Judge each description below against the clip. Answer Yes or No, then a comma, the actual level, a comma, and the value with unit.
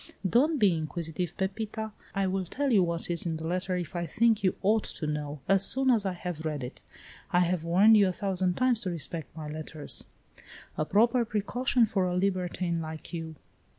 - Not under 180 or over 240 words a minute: Yes, average, 200 wpm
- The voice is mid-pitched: Yes, medium, 180 Hz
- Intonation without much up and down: No, average, 4.2 semitones